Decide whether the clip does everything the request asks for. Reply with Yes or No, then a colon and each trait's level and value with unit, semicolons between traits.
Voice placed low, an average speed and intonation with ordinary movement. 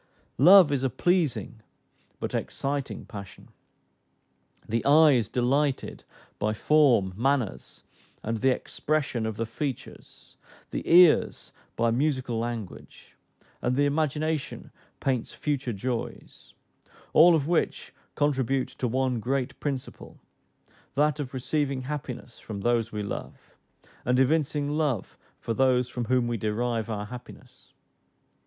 No: low, 130 Hz; slow, 120 wpm; average, 3.8 semitones